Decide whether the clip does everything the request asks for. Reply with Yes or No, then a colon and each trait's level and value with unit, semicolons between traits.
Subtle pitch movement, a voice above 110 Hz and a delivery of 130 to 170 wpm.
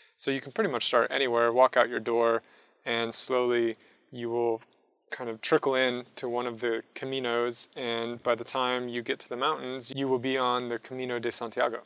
No: narrow, 1.5 semitones; low, 120 Hz; fast, 205 wpm